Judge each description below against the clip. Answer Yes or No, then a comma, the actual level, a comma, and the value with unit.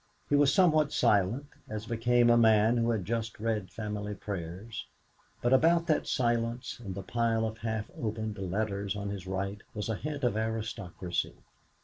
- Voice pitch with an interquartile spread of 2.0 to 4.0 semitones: Yes, narrow, 2.5 semitones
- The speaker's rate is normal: Yes, average, 165 wpm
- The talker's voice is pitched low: Yes, low, 110 Hz